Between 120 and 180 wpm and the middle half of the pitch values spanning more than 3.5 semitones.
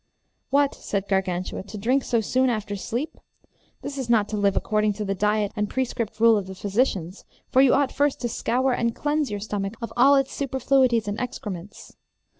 No: average, 195 wpm; average, 4.3 semitones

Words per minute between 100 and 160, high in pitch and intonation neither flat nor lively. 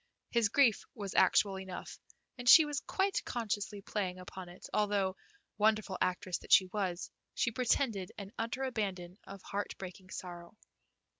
Yes: average, 150 wpm; high, 200 Hz; average, 3.4 semitones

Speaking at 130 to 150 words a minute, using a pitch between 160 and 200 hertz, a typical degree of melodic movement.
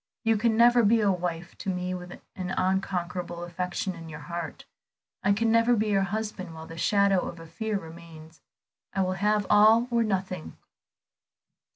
No: average, 175 wpm; high, 190 Hz; average, 3.7 semitones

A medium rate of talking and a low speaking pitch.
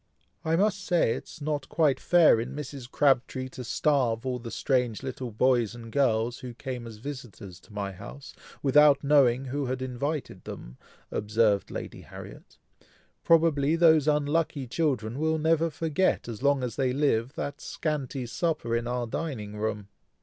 Yes: average, 165 wpm; low, 130 Hz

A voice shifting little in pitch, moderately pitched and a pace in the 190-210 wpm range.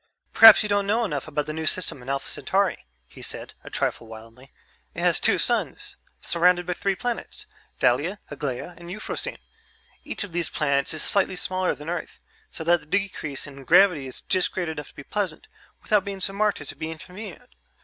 No: average, 5.1 semitones; medium, 175 Hz; average, 200 wpm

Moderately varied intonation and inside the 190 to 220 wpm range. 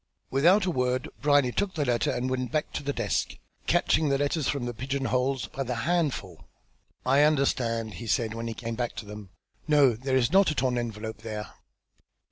Yes: average, 3.7 semitones; average, 200 wpm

